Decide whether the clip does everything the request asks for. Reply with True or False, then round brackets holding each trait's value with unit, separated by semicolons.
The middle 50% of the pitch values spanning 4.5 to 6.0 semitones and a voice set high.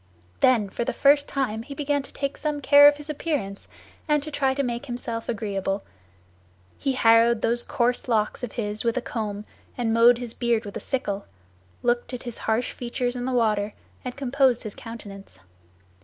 False (3.4 semitones; 240 Hz)